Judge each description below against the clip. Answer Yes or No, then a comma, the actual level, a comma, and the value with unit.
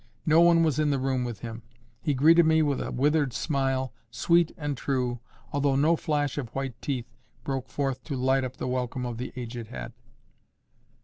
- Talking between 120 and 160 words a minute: No, average, 190 wpm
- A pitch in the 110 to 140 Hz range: Yes, low, 135 Hz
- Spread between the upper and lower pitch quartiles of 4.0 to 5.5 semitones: No, average, 2.9 semitones